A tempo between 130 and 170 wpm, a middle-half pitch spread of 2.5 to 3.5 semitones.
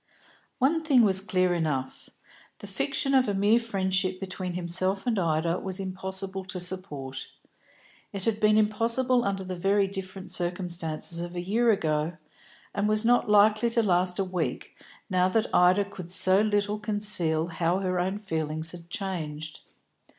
Yes: average, 160 wpm; average, 3.0 semitones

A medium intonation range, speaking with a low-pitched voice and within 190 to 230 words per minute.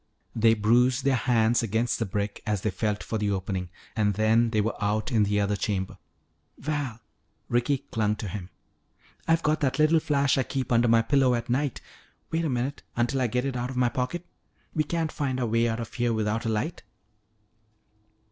Yes: average, 3.6 semitones; low, 120 Hz; average, 200 wpm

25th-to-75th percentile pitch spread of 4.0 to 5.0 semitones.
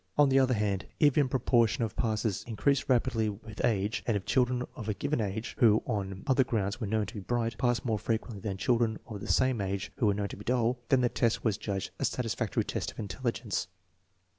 No: average, 3.2 semitones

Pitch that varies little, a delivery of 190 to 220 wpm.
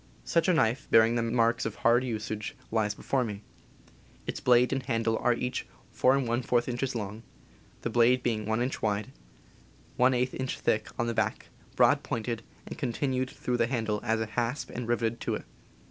No: narrow, 2.0 semitones; average, 175 wpm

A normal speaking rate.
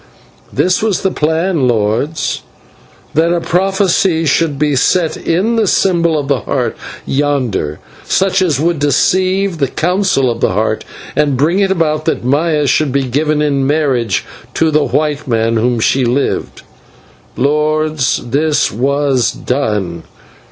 Yes: average, 145 wpm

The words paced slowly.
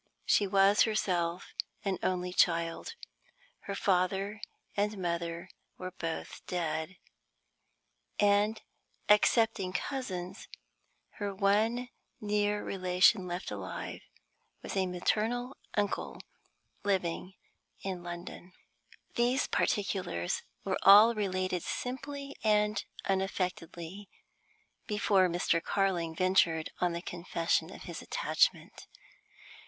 Yes: slow, 95 wpm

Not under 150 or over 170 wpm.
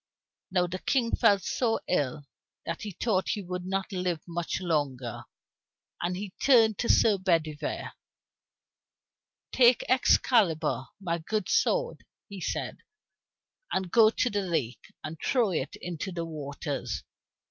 No: average, 140 wpm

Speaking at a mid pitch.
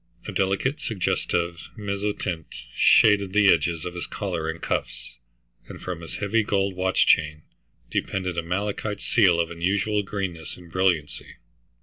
No: very low, 95 Hz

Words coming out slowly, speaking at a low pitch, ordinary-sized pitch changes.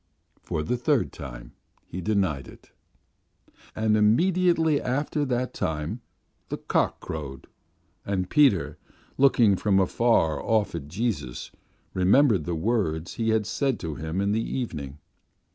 No: slow, 130 wpm; low, 100 Hz; wide, 7.3 semitones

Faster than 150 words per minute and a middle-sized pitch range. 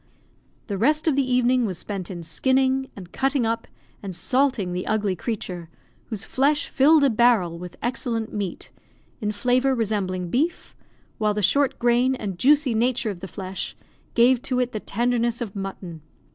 Yes: average, 170 wpm; average, 5.0 semitones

